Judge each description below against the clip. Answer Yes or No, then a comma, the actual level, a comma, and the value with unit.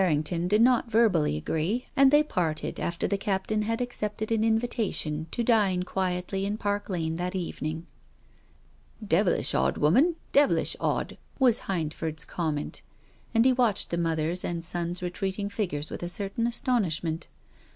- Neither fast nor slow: Yes, average, 160 wpm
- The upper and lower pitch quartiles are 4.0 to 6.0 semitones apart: Yes, average, 5.2 semitones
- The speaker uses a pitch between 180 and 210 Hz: Yes, high, 190 Hz